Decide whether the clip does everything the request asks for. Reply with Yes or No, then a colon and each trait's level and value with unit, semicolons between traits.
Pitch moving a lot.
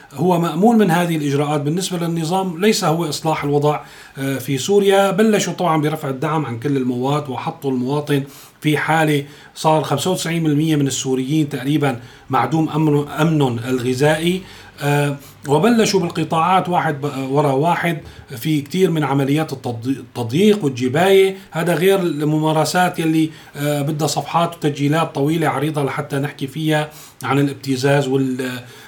No: average, 3.0 semitones